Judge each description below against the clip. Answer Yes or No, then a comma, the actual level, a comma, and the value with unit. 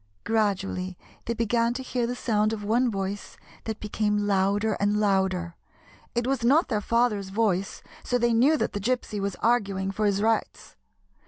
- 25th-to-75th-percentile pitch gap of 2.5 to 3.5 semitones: Yes, average, 2.9 semitones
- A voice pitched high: Yes, high, 210 Hz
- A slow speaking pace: No, average, 170 wpm